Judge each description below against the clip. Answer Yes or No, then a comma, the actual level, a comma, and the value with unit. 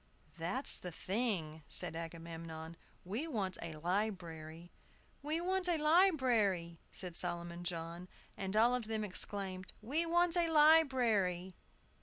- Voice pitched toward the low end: No, high, 190 Hz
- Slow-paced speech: Yes, slow, 125 wpm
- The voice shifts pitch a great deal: Yes, wide, 7.4 semitones